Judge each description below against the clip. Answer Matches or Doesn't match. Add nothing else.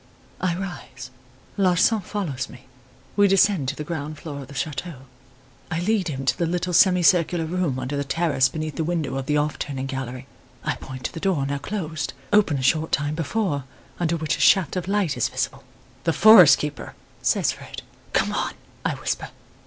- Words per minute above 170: Matches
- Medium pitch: Matches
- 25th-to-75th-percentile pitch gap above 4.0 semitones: Matches